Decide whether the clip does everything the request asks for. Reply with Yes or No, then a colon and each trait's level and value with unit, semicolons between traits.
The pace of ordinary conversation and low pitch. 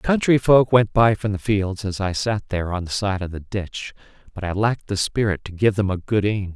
No: fast, 255 wpm; low, 100 Hz